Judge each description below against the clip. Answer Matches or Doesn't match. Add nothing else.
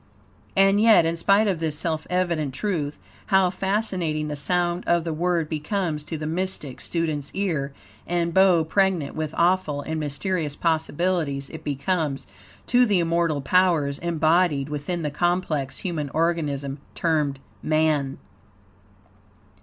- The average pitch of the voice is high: Doesn't match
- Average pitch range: Matches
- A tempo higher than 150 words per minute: Doesn't match